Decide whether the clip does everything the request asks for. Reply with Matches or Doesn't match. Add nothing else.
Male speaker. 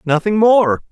Matches